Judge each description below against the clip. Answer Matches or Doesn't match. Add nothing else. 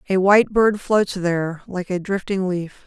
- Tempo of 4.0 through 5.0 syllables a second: Matches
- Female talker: Matches